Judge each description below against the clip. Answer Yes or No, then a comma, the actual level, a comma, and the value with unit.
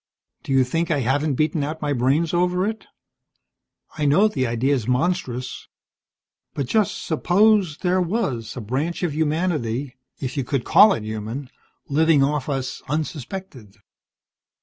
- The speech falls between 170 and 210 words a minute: No, average, 145 wpm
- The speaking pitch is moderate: Yes, medium, 145 Hz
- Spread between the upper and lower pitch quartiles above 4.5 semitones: Yes, average, 5.1 semitones